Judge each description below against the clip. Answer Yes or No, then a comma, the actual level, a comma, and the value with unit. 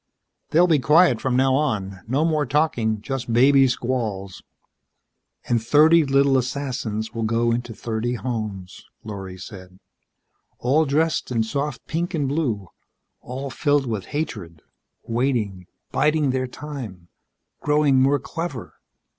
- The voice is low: Yes, low, 130 Hz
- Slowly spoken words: Yes, slow, 130 wpm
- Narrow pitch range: No, average, 4.8 semitones